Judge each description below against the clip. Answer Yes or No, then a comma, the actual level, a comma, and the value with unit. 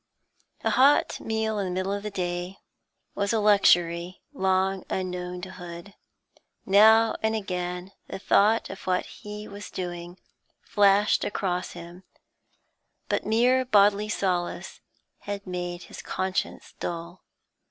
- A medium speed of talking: No, slow, 125 wpm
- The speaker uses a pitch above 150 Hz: Yes, high, 190 Hz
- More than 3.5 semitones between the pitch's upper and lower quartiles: No, average, 2.7 semitones